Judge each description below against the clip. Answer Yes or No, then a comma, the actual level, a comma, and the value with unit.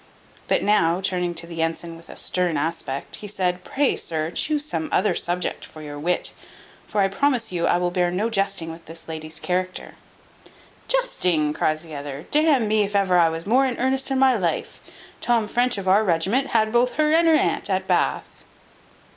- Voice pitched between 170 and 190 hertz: Yes, medium, 185 Hz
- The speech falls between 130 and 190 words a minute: No, average, 200 wpm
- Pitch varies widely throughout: Yes, wide, 6.4 semitones